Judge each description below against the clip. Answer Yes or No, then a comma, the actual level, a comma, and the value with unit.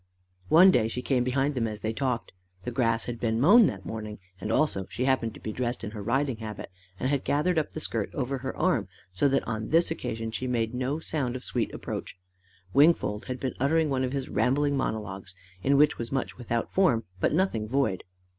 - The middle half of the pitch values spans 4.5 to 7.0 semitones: No, average, 4.0 semitones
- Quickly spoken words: Yes, fast, 215 wpm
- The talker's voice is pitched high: No, low, 125 Hz